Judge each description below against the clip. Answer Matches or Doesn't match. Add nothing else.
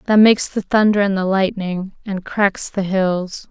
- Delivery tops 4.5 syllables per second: Doesn't match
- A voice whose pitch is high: Matches